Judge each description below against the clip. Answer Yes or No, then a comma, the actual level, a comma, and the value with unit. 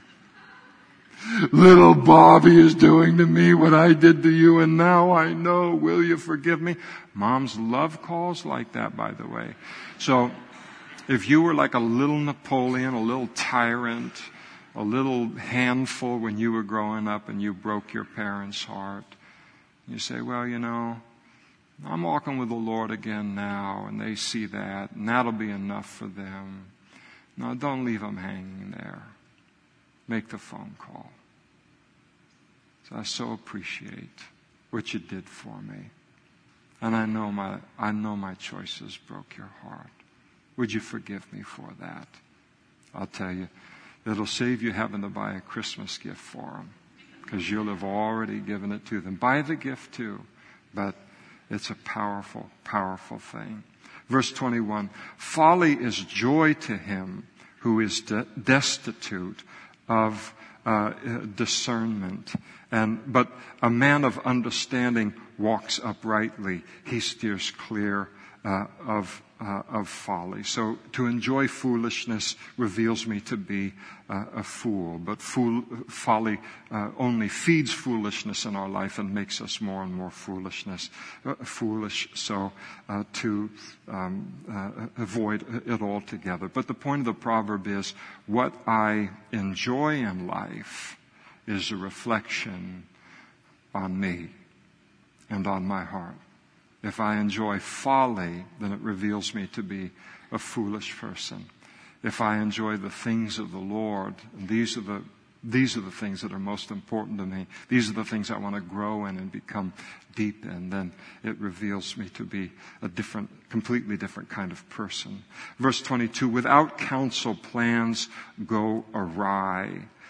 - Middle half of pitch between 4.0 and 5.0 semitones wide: No, average, 3.5 semitones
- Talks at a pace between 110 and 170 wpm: Yes, average, 150 wpm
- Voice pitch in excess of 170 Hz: No, low, 110 Hz